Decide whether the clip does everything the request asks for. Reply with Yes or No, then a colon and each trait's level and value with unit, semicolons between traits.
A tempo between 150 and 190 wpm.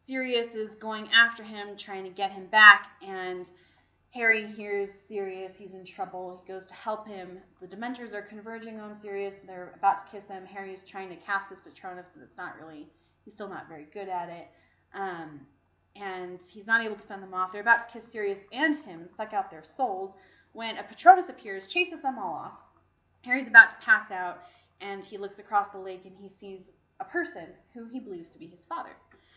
No: fast, 205 wpm